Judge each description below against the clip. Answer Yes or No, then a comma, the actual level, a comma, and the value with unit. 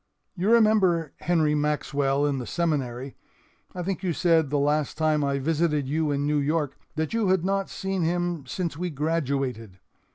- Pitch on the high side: No, medium, 155 Hz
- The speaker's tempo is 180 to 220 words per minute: No, average, 170 wpm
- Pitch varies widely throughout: No, average, 3.6 semitones